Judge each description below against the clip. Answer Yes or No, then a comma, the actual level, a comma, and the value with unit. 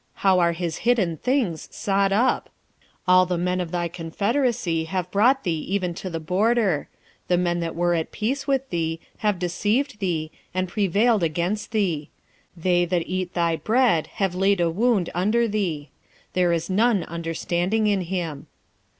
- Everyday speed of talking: Yes, average, 165 wpm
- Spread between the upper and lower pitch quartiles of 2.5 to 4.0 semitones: Yes, average, 3.7 semitones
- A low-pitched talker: No, medium, 185 Hz